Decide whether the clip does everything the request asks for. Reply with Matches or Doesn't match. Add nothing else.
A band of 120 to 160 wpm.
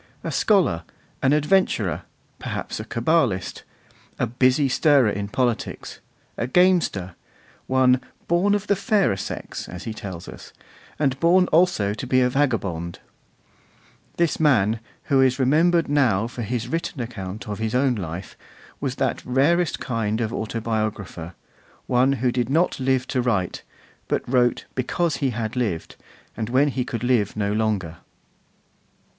Matches